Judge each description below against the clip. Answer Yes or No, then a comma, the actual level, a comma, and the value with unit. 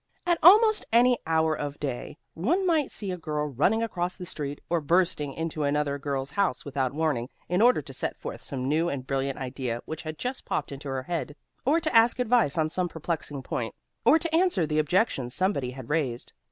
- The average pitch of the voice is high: No, medium, 155 Hz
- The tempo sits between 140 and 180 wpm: No, fast, 205 wpm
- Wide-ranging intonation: Yes, wide, 6.7 semitones